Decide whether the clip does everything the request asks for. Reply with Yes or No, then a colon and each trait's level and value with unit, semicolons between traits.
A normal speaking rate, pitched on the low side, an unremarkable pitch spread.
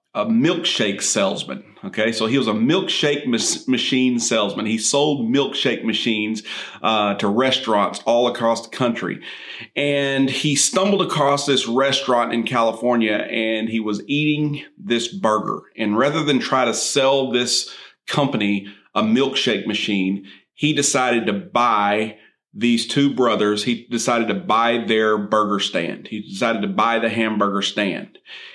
Yes: average, 145 wpm; low, 115 Hz; average, 3.9 semitones